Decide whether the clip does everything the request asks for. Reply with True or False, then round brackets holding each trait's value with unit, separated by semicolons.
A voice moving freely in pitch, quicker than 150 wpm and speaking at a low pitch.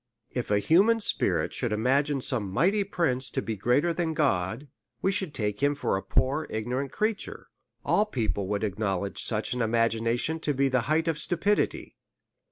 True (6.7 semitones; 175 wpm; 130 Hz)